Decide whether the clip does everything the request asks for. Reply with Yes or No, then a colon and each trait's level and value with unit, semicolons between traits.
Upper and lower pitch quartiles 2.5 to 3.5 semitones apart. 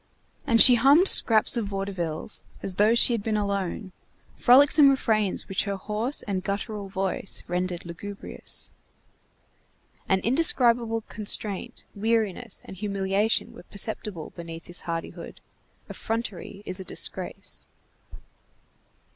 Yes: average, 3.1 semitones